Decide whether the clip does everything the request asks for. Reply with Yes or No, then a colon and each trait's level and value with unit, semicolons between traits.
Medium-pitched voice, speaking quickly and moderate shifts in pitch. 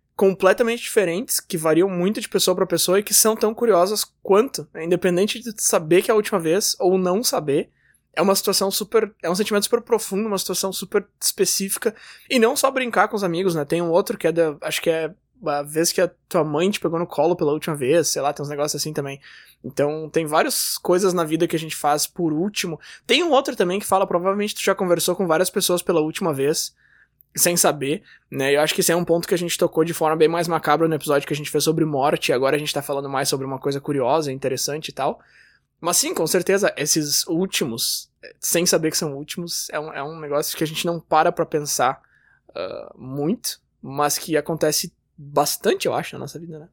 Yes: medium, 170 Hz; fast, 230 wpm; average, 4.3 semitones